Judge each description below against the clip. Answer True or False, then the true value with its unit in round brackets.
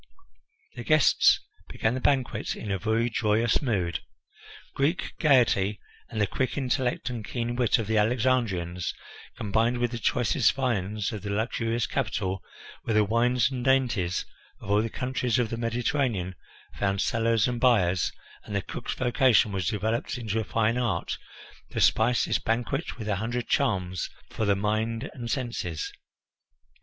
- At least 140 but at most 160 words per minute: True (155 wpm)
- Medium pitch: False (115 Hz)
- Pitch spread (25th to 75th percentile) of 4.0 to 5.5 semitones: False (3.2 semitones)